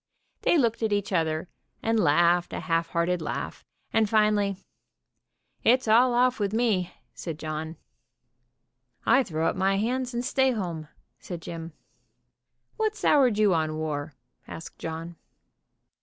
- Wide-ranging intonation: Yes, wide, 5.7 semitones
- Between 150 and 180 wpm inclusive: No, average, 140 wpm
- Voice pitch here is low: No, high, 195 Hz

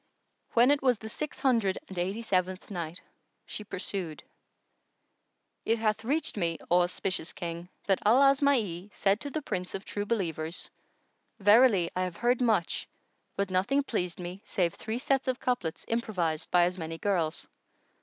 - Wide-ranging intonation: No, average, 4.9 semitones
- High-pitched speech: Yes, high, 200 Hz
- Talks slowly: No, average, 160 wpm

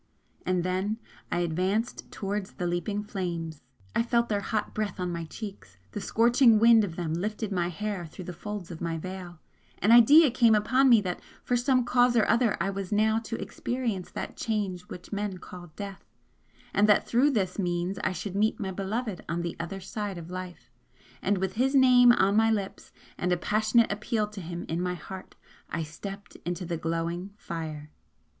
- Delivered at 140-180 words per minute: No, average, 190 wpm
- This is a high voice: Yes, high, 195 Hz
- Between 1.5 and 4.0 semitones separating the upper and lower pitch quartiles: Yes, average, 3.7 semitones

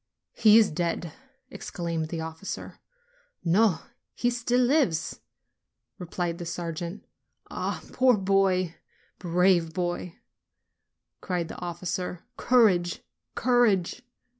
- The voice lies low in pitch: No, medium, 180 Hz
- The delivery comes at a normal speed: No, slow, 100 wpm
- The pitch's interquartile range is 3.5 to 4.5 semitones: Yes, average, 4.0 semitones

